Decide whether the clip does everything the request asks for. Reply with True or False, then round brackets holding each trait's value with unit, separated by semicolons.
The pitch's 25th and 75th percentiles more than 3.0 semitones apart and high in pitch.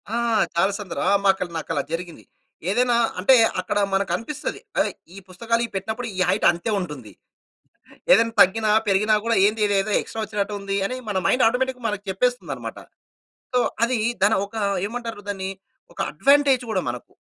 True (3.5 semitones; 210 Hz)